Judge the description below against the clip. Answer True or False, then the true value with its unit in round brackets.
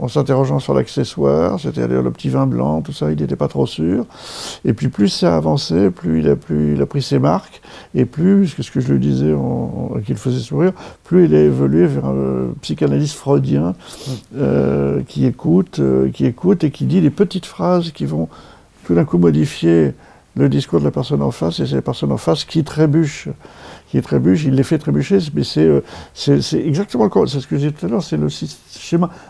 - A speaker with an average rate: False (225 wpm)